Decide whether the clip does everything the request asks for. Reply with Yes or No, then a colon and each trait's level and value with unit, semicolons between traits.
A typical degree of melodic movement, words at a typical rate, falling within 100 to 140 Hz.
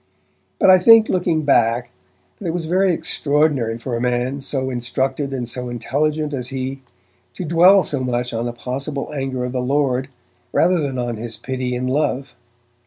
Yes: average, 3.5 semitones; average, 175 wpm; low, 135 Hz